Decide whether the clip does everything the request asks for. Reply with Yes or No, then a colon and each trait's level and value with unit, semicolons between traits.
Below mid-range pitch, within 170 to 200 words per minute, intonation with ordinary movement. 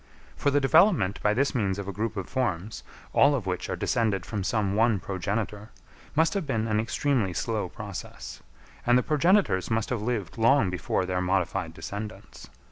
Yes: low, 110 Hz; average, 180 wpm; average, 4.5 semitones